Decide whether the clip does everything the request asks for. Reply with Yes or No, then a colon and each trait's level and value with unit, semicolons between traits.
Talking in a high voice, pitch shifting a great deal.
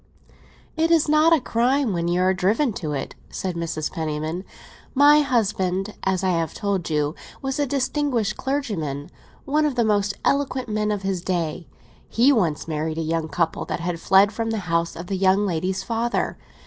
Yes: high, 195 Hz; wide, 6.7 semitones